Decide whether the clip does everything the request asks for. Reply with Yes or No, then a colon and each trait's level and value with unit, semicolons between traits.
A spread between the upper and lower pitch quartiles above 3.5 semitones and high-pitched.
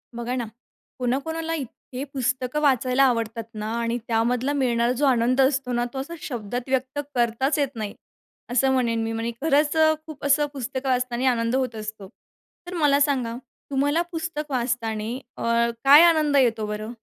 No: average, 3.2 semitones; very high, 255 Hz